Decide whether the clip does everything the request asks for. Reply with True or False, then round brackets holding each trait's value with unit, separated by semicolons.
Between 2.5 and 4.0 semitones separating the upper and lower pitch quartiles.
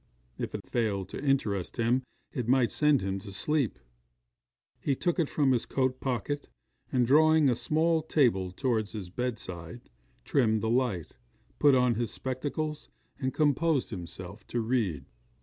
False (5.2 semitones)